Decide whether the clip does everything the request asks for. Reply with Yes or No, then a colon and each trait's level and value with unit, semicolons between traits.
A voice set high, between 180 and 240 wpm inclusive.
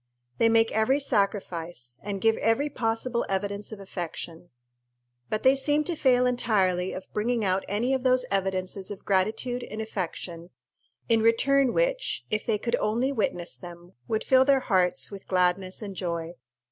No: high, 215 Hz; average, 160 wpm